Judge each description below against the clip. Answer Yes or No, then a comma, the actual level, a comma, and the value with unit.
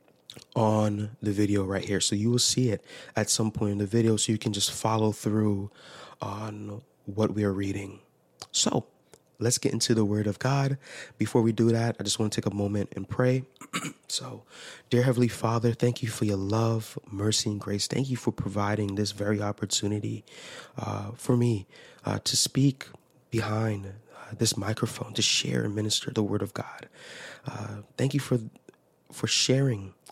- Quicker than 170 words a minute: Yes, average, 180 wpm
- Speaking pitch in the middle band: No, low, 110 Hz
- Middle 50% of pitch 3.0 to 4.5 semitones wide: No, narrow, 2.6 semitones